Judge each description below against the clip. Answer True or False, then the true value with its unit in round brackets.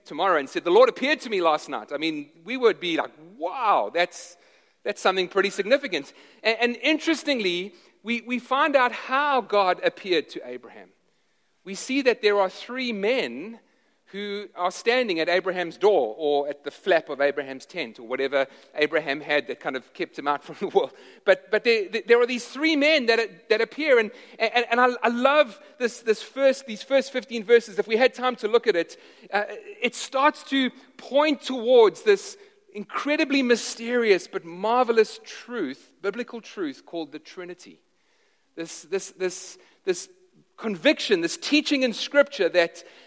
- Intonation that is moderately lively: False (7.1 semitones)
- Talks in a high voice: True (235 Hz)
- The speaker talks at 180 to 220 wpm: False (170 wpm)